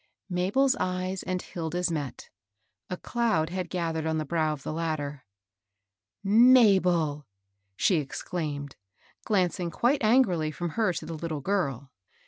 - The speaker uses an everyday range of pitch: Yes, average, 3.5 semitones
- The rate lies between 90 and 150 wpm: Yes, average, 145 wpm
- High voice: No, medium, 170 Hz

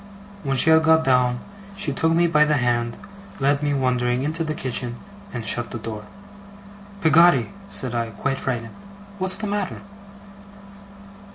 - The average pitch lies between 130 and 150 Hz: Yes, low, 135 Hz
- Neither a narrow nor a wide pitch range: Yes, average, 4.7 semitones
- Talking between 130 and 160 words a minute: Yes, average, 155 wpm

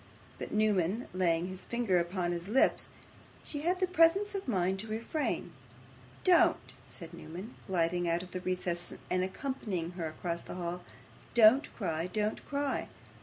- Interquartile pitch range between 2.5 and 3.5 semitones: No, wide, 5.6 semitones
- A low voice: No, medium, 185 Hz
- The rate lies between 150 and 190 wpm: Yes, average, 155 wpm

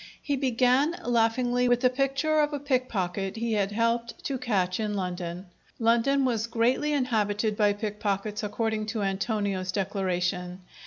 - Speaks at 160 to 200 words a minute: No, average, 145 wpm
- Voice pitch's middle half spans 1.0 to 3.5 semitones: No, average, 4.1 semitones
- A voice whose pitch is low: No, high, 225 Hz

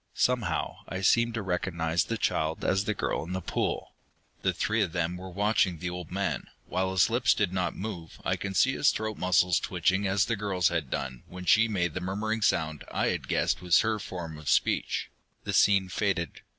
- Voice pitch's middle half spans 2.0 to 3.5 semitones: Yes, average, 3.0 semitones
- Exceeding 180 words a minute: Yes, fast, 205 wpm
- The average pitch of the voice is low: Yes, very low, 95 Hz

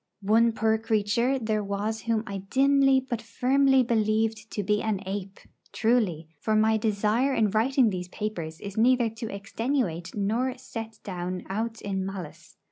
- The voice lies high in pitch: Yes, high, 220 Hz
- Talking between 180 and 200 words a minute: No, average, 155 wpm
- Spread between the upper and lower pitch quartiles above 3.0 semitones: No, average, 2.7 semitones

